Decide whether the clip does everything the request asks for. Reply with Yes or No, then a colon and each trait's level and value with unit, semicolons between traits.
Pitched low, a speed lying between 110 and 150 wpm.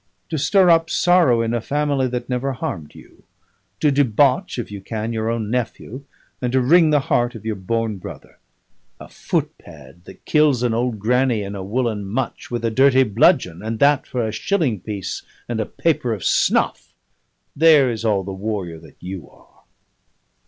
No: low, 115 Hz; average, 180 wpm